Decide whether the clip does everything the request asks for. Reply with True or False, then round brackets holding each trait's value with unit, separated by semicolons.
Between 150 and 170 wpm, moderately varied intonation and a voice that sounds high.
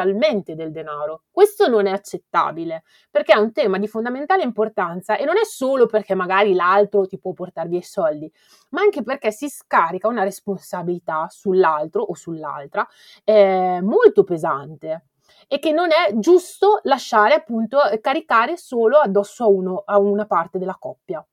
False (155 wpm; 6.9 semitones; 205 Hz)